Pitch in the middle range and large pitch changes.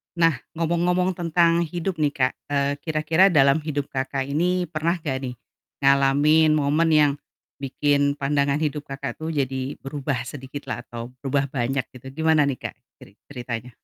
No: medium, 145 Hz; average, 2.8 semitones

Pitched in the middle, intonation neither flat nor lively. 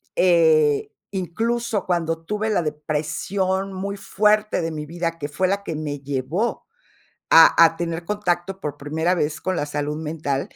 Yes: medium, 170 Hz; average, 4.2 semitones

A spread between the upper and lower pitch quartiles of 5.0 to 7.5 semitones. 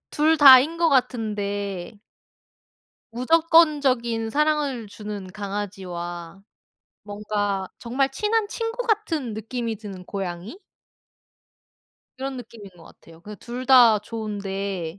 Yes: wide, 5.5 semitones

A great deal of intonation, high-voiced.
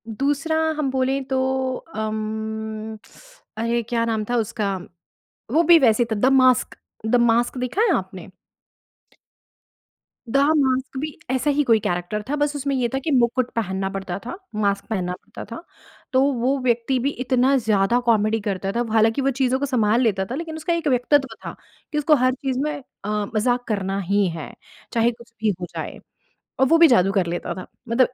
No: average, 3.9 semitones; high, 240 Hz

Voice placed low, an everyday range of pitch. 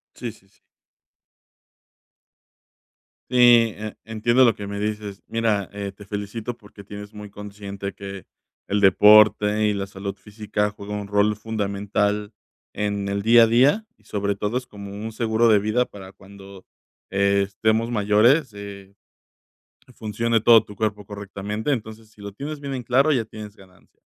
No: low, 105 Hz; narrow, 1.8 semitones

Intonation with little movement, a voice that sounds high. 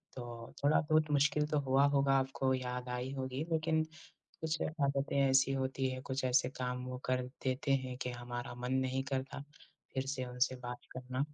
No: narrow, 1.8 semitones; low, 130 Hz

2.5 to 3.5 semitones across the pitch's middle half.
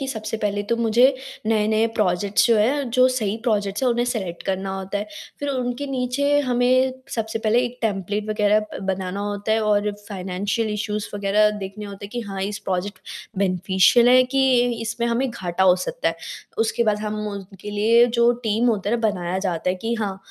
Yes: average, 3.0 semitones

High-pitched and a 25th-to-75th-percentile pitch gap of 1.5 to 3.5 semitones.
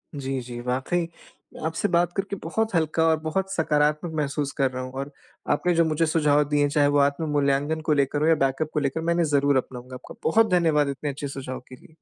No: medium, 150 Hz; average, 2.8 semitones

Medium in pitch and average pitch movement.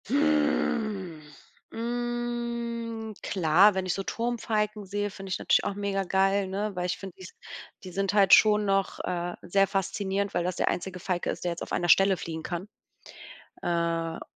No: high, 195 Hz; average, 3.0 semitones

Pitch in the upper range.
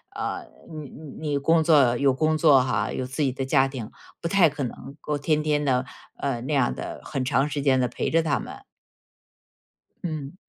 No: medium, 140 Hz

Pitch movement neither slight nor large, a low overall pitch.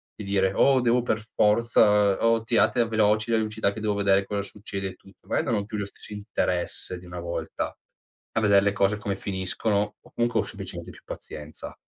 No: narrow, 2.1 semitones; low, 105 Hz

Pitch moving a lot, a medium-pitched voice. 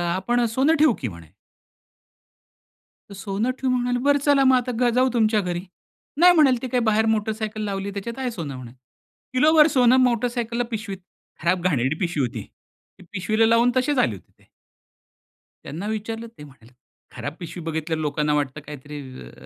No: wide, 7.8 semitones; high, 215 Hz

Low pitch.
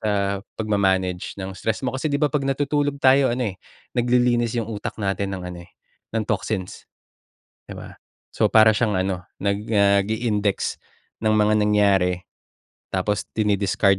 Yes: low, 105 Hz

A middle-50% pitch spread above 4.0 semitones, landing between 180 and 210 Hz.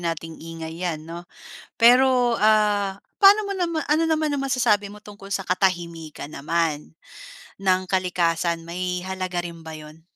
Yes: average, 4.5 semitones; medium, 185 Hz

